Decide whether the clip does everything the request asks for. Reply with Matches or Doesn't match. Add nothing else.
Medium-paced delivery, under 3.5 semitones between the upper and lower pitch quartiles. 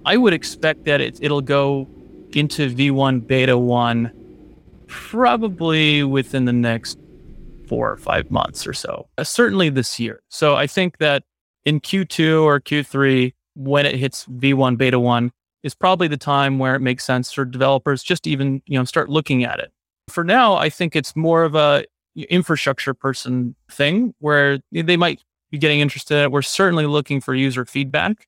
Matches